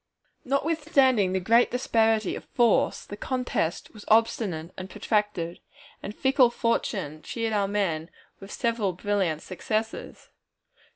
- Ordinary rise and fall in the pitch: Yes, average, 4.0 semitones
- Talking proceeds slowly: Yes, slow, 120 wpm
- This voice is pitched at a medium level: No, high, 210 Hz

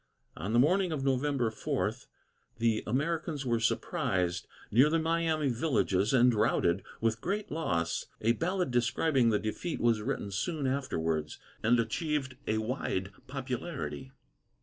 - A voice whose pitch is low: Yes, low, 125 Hz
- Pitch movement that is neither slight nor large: No, wide, 5.7 semitones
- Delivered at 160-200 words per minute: No, slow, 135 wpm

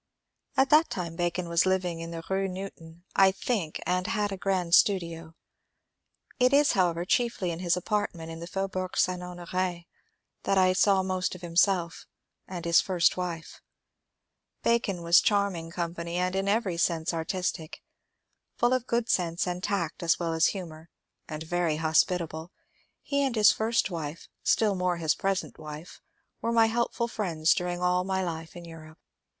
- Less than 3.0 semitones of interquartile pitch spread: Yes, narrow, 2.6 semitones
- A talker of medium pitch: Yes, medium, 180 Hz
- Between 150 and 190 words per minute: Yes, average, 170 wpm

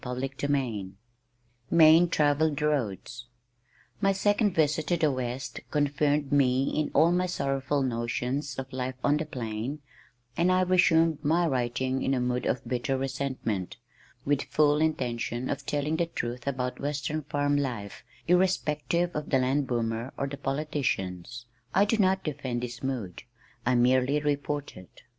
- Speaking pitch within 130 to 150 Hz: Yes, medium, 140 Hz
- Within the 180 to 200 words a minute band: No, average, 150 wpm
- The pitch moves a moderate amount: Yes, average, 3.5 semitones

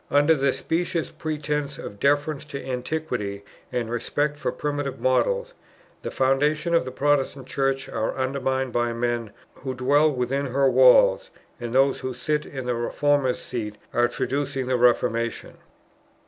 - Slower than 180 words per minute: Yes, average, 145 wpm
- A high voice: No, low, 135 Hz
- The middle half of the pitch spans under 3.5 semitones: Yes, average, 2.9 semitones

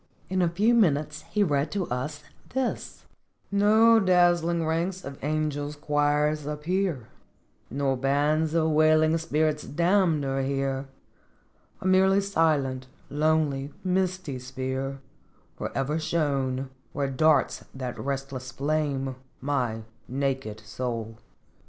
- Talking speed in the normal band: No, slow, 115 wpm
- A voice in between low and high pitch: Yes, medium, 150 Hz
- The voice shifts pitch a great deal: No, average, 3.6 semitones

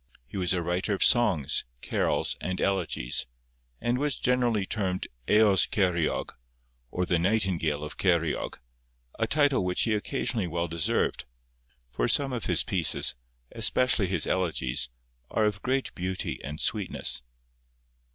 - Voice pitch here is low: Yes, very low, 95 Hz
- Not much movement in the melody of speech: No, average, 4.5 semitones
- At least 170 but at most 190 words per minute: No, slow, 135 wpm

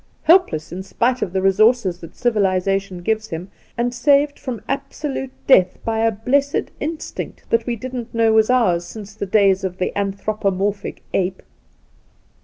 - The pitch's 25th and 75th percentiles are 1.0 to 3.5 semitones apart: No, average, 4.4 semitones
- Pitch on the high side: Yes, high, 215 Hz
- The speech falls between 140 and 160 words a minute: Yes, average, 155 wpm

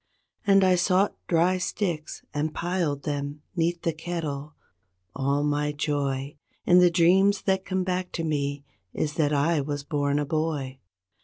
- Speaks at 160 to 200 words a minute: No, average, 150 wpm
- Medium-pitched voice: Yes, medium, 155 Hz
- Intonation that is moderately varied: Yes, average, 3.7 semitones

